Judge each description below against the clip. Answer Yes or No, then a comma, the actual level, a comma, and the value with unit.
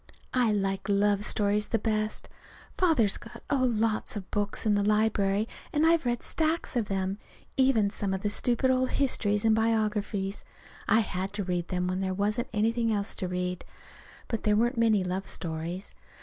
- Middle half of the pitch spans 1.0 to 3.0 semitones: Yes, average, 2.7 semitones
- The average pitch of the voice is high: Yes, high, 210 Hz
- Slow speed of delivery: No, average, 175 wpm